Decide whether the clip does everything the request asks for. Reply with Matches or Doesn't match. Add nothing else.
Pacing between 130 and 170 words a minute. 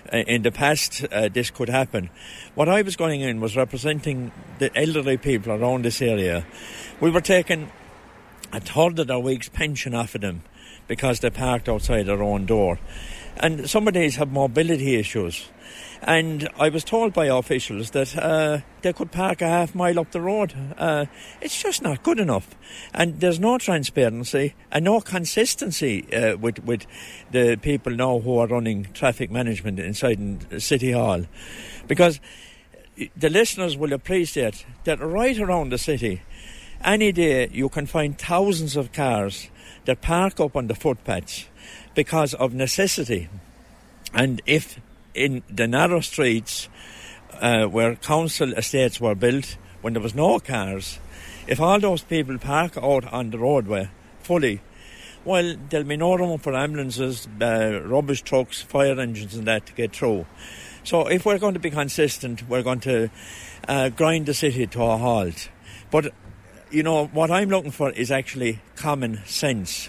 Matches